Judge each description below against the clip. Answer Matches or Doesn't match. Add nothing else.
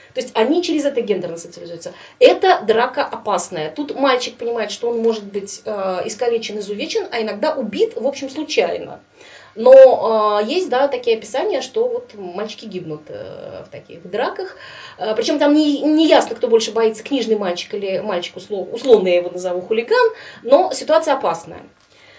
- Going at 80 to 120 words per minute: Doesn't match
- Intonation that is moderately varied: Doesn't match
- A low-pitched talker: Doesn't match